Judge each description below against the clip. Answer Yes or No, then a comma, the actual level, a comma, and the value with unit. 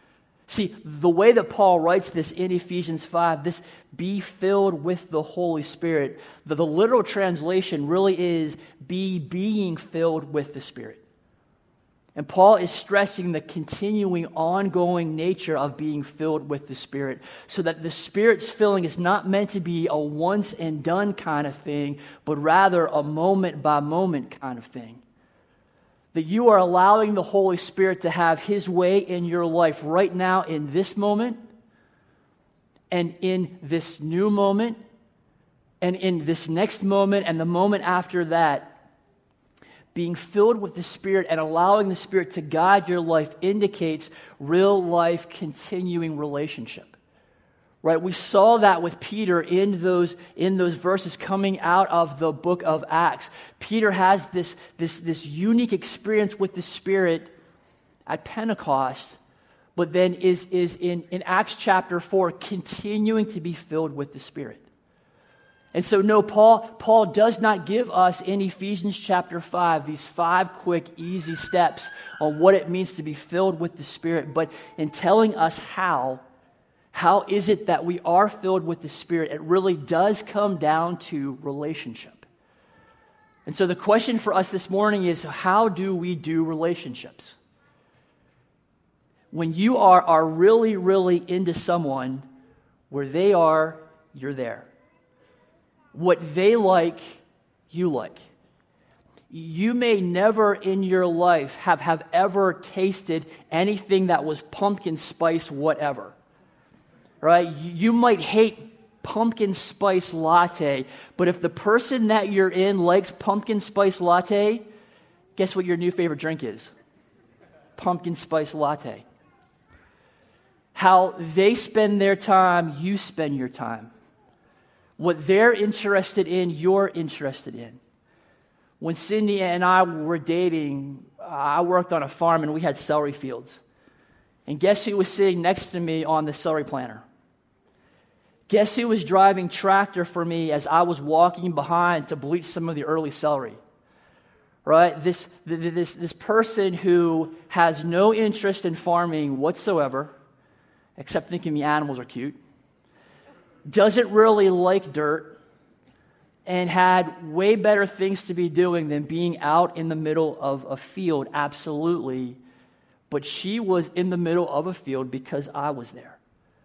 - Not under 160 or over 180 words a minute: No, average, 145 wpm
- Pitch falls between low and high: Yes, medium, 175 Hz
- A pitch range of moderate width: Yes, average, 3.4 semitones